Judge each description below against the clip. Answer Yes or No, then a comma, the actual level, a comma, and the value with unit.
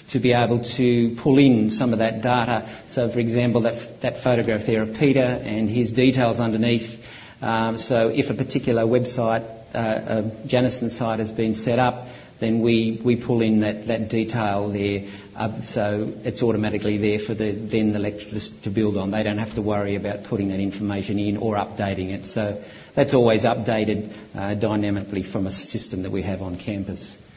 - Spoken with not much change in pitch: Yes, narrow, 2.3 semitones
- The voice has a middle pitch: No, low, 110 Hz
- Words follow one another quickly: No, average, 190 wpm